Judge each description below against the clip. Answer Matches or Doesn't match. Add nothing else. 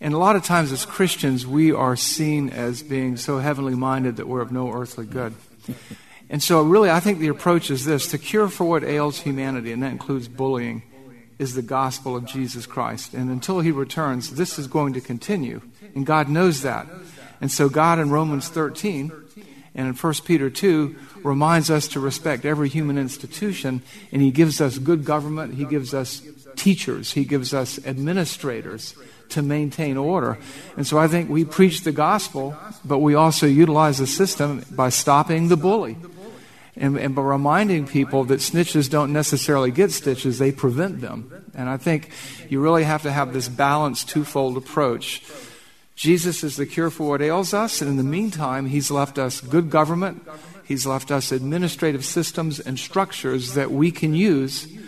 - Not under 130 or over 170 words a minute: Doesn't match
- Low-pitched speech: Doesn't match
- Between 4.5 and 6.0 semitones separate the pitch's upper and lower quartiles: Doesn't match